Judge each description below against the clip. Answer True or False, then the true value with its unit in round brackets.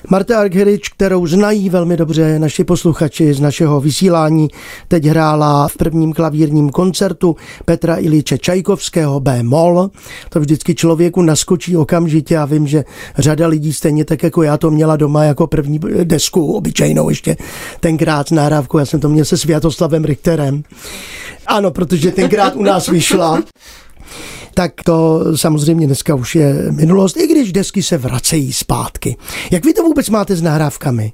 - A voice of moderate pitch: True (165 Hz)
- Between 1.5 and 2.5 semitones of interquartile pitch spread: False (2.9 semitones)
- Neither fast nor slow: True (150 wpm)